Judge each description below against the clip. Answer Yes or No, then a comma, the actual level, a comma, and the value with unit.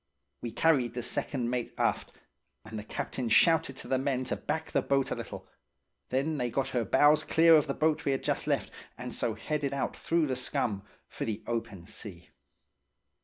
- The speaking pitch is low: Yes, low, 130 Hz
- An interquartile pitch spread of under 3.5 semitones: No, average, 4.2 semitones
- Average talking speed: Yes, average, 195 wpm